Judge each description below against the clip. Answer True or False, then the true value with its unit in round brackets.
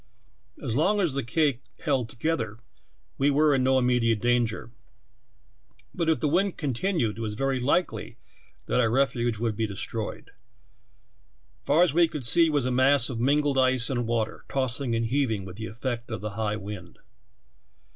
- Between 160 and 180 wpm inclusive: True (170 wpm)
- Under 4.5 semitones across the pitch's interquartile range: True (4.0 semitones)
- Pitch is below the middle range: True (125 Hz)